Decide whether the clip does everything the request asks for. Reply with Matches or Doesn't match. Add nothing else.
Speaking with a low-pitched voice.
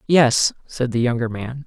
Matches